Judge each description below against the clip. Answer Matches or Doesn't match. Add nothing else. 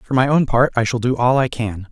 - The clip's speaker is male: Matches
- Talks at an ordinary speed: Doesn't match